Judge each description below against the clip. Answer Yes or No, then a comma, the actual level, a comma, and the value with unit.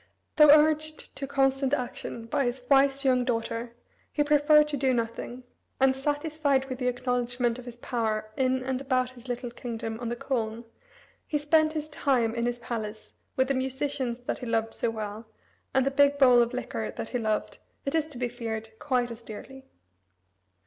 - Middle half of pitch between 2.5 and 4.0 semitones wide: Yes, average, 2.8 semitones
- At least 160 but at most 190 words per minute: Yes, average, 185 wpm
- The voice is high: Yes, very high, 255 Hz